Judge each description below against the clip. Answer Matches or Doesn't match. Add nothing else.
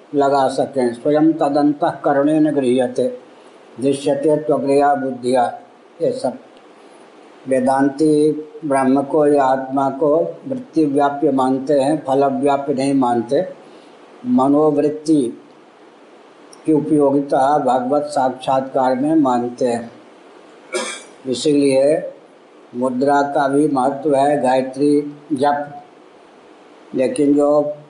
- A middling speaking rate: Doesn't match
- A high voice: Doesn't match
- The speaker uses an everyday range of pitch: Doesn't match